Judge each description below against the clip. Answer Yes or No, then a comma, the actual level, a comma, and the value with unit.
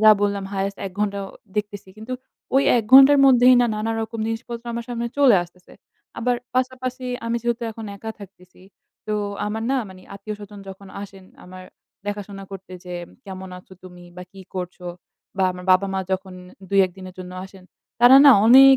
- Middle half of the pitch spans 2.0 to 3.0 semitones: No, average, 3.8 semitones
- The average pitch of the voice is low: No, high, 205 Hz